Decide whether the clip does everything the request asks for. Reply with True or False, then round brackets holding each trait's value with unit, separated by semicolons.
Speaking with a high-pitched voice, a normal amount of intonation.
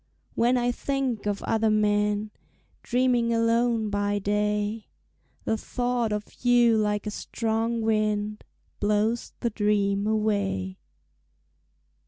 False (215 Hz; 2.0 semitones)